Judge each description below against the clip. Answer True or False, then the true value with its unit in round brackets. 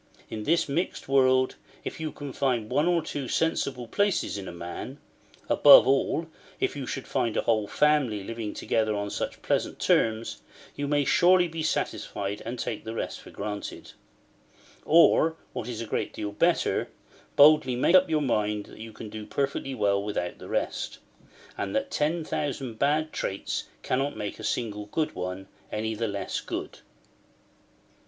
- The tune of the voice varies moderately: False (5.9 semitones)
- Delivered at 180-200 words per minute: False (165 wpm)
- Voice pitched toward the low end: True (120 Hz)